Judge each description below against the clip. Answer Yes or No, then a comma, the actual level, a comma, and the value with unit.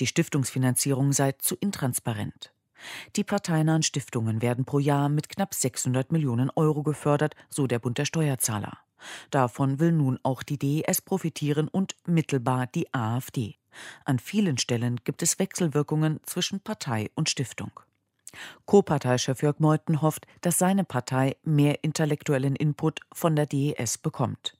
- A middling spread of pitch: Yes, average, 3.3 semitones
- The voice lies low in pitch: No, medium, 145 Hz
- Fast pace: No, average, 140 wpm